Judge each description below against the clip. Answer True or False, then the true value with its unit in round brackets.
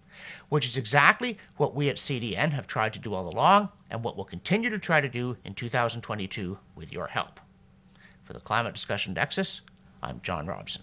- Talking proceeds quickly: False (190 wpm)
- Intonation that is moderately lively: False (5.9 semitones)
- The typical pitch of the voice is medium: False (125 Hz)